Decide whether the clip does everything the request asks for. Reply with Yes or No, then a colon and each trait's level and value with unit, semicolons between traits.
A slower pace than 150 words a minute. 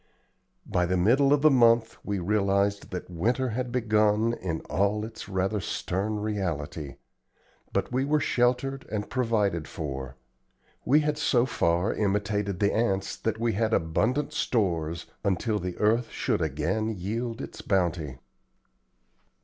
Yes: average, 140 wpm